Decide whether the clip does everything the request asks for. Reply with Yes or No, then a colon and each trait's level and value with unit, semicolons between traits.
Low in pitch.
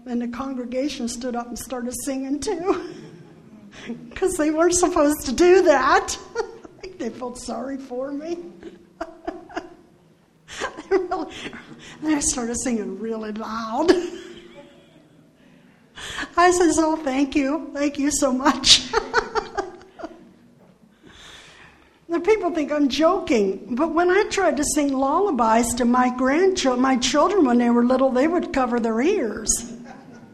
No: very high, 290 Hz